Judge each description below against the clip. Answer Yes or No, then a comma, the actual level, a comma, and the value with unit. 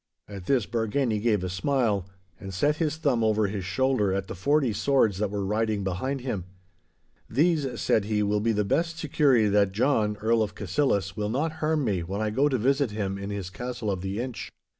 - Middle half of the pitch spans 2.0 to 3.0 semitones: No, average, 5.1 semitones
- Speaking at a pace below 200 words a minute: No, fast, 205 wpm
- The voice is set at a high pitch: No, low, 110 Hz